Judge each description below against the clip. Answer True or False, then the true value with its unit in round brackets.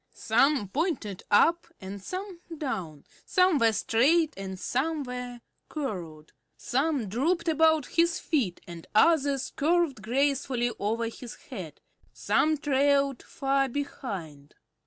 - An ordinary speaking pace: False (115 wpm)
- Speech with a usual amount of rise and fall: False (6.2 semitones)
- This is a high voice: True (270 Hz)